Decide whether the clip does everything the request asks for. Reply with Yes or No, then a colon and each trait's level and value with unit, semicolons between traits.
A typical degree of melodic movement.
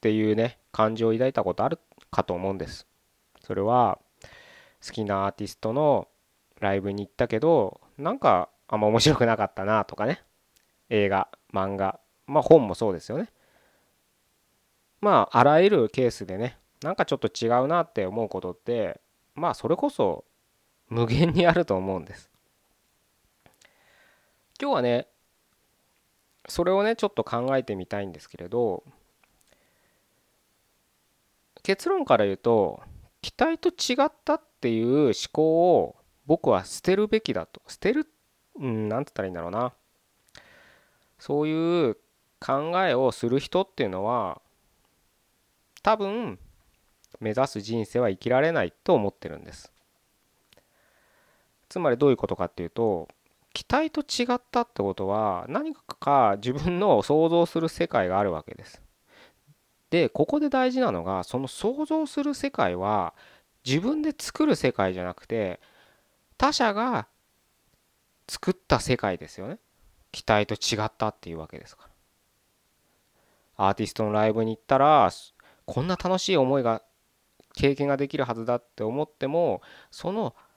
No: wide, 8.8 semitones